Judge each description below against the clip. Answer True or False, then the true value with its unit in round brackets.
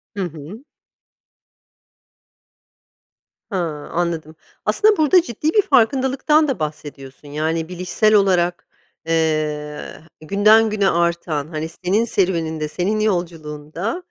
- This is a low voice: False (175 Hz)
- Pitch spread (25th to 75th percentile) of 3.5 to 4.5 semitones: False (5.6 semitones)